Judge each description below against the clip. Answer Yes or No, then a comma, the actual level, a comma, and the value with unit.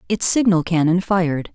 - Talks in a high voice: No, medium, 175 Hz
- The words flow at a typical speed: Yes, average, 155 wpm